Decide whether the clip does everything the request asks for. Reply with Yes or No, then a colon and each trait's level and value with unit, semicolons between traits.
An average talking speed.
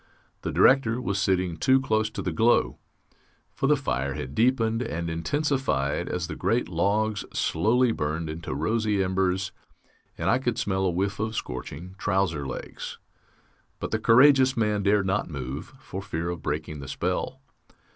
Yes: average, 160 wpm